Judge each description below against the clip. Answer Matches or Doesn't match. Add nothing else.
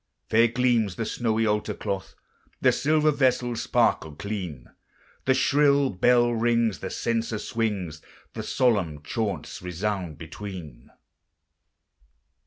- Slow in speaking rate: Matches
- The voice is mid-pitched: Doesn't match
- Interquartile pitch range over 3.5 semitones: Matches